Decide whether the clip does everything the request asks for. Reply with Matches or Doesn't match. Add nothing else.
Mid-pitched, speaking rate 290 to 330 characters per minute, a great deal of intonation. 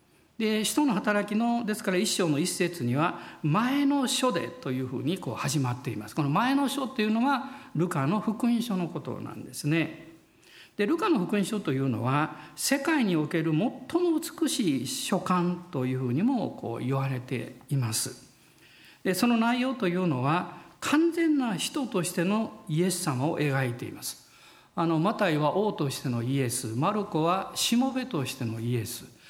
Matches